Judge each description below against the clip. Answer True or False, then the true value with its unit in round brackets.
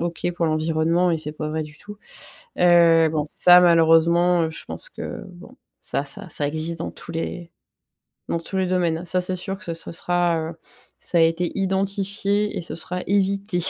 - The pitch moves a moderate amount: False (2.1 semitones)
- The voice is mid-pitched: True (170 Hz)